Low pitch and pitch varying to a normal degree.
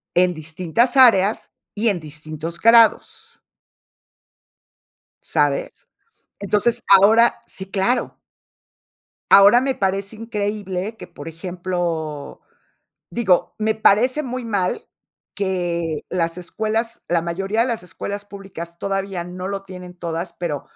No: high, 195 Hz; average, 4.1 semitones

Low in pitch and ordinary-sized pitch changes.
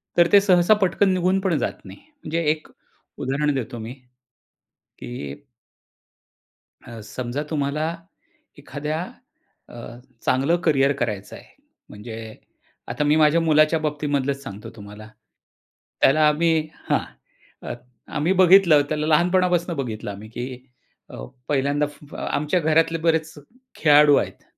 No: medium, 150 Hz; average, 3.7 semitones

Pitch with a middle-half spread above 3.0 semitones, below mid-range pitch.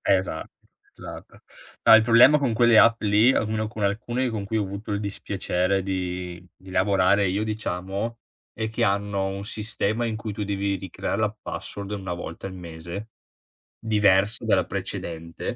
No: narrow, 2.5 semitones; low, 100 Hz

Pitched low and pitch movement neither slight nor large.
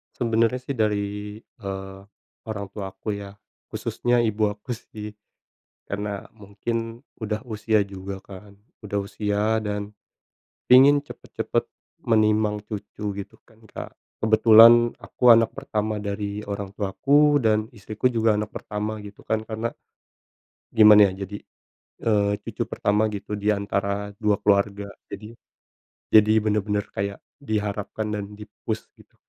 No: low, 105 Hz; narrow, 1.4 semitones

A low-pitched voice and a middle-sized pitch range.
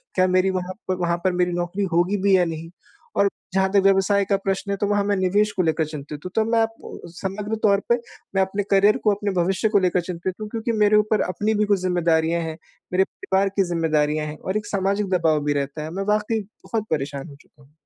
No: high, 190 Hz; average, 3.3 semitones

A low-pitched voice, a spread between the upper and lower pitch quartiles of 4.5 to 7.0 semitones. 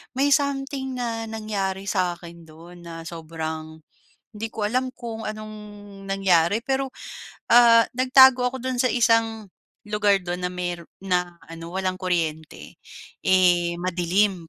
No: high, 195 Hz; average, 5.0 semitones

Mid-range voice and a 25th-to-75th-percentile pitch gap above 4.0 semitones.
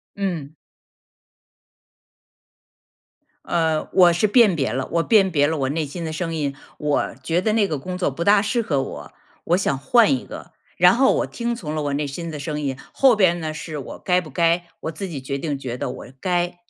Yes: medium, 165 Hz; average, 4.4 semitones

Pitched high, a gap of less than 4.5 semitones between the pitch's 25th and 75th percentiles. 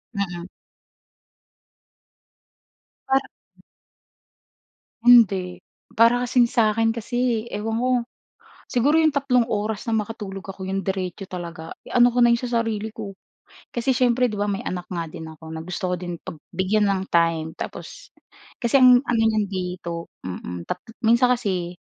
No: high, 210 Hz; average, 4.8 semitones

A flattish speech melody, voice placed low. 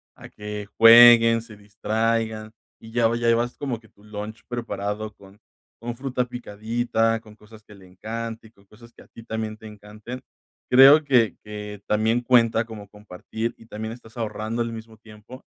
Yes: narrow, 1.7 semitones; low, 110 Hz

